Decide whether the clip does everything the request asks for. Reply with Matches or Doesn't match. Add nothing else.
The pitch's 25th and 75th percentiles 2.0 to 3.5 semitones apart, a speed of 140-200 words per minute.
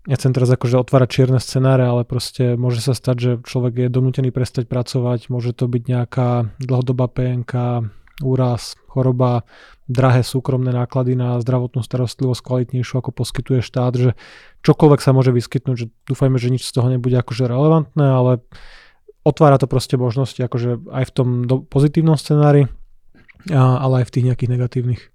Doesn't match